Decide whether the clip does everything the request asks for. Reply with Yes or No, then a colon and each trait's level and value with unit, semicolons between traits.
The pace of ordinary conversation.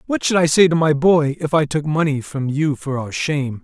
No: fast, 265 wpm